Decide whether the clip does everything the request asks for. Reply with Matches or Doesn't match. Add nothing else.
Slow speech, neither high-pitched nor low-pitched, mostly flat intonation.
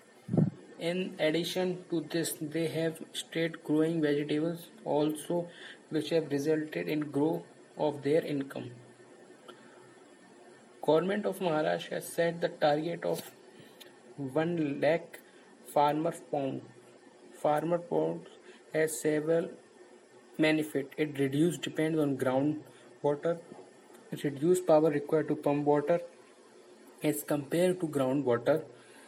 Matches